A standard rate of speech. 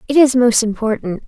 Yes: average, 190 wpm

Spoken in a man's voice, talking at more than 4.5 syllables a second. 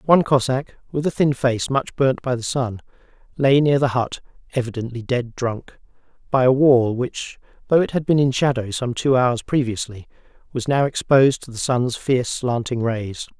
Yes: male; 4.9 syllables/s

